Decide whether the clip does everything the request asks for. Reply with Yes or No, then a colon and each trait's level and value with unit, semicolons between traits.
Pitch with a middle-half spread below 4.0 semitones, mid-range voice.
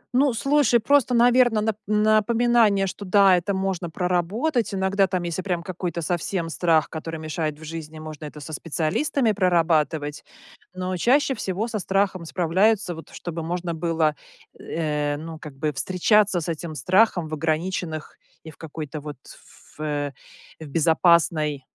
No: average, 4.4 semitones; medium, 175 Hz